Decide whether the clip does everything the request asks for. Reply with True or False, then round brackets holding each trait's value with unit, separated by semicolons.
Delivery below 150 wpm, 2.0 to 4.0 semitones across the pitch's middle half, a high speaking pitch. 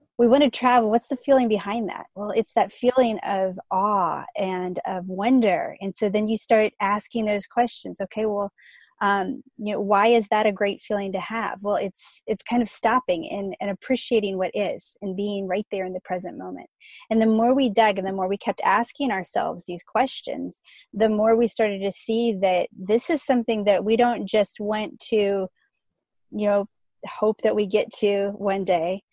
False (200 wpm; 2.8 semitones; 210 Hz)